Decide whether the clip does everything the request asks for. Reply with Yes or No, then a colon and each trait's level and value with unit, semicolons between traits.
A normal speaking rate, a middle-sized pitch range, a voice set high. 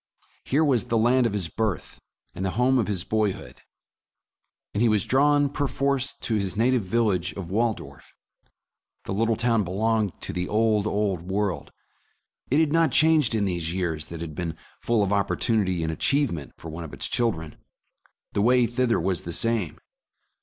No: average, 180 wpm; average, 4.8 semitones; low, 105 Hz